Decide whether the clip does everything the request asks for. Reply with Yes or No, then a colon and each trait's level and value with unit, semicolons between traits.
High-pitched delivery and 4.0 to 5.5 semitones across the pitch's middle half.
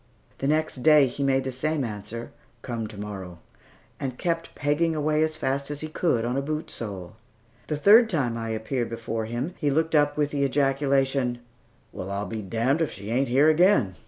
No: low, 135 Hz; average, 4.8 semitones